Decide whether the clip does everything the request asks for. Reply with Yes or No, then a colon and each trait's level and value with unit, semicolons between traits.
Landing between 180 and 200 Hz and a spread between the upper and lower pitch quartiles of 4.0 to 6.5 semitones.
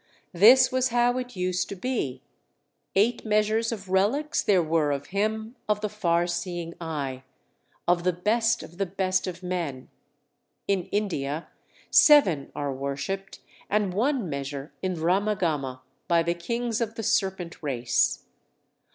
Yes: medium, 185 Hz; average, 4.7 semitones